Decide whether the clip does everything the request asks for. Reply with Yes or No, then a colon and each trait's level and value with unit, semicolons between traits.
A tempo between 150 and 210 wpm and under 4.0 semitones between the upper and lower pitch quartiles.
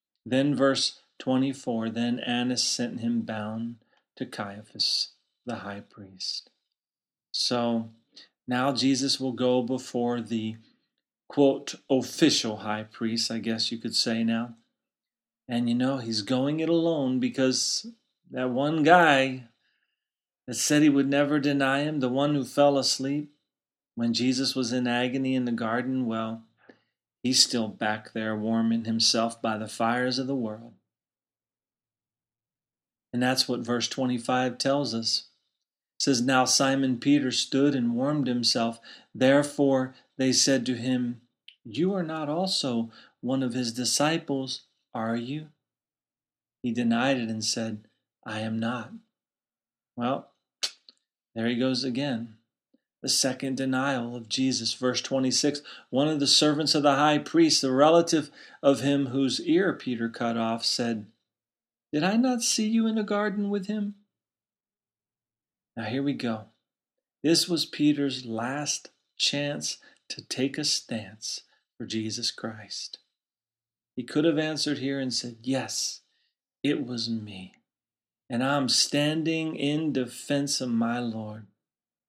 No: average, 140 wpm; average, 3.6 semitones